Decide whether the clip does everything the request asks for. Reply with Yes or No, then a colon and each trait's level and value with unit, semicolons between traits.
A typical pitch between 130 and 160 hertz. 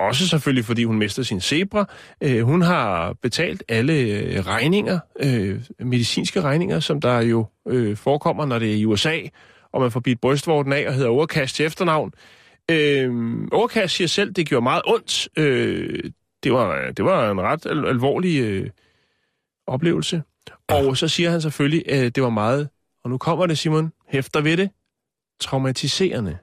Yes: low, 135 Hz